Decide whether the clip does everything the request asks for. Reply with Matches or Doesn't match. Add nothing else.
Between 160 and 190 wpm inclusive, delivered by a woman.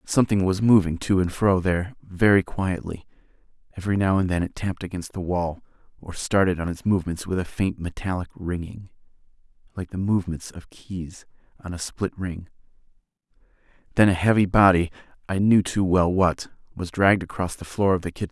Doesn't match